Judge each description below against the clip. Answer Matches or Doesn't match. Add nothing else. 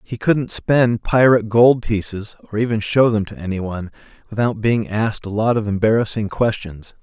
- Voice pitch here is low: Matches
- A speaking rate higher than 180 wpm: Doesn't match